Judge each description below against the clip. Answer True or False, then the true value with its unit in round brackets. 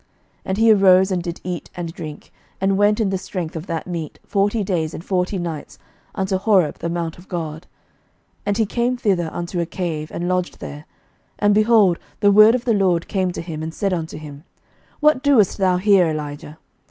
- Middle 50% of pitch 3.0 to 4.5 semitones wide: True (3.5 semitones)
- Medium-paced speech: False (210 wpm)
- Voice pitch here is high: False (180 Hz)